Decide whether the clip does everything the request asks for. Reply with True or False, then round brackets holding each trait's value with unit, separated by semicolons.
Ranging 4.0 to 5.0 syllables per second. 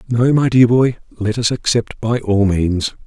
True (4.4 syllables/s)